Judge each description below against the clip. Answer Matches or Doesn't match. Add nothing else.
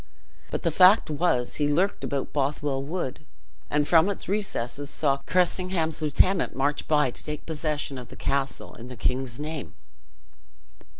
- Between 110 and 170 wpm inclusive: Matches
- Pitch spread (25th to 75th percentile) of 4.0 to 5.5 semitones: Doesn't match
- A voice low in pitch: Doesn't match